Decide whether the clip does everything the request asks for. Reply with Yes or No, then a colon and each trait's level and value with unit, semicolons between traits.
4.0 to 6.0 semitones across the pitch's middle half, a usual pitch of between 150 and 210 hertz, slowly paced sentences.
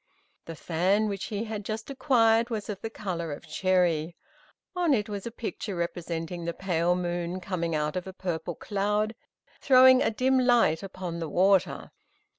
No: average, 4.4 semitones; high, 190 Hz; average, 170 wpm